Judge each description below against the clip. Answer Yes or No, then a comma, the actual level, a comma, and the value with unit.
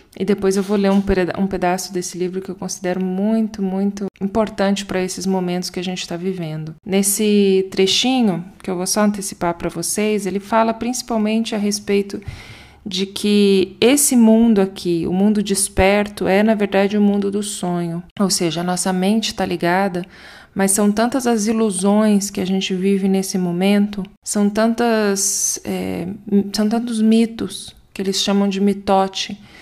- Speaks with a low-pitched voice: No, high, 195 Hz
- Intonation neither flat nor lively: No, narrow, 1.9 semitones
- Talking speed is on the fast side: No, average, 165 wpm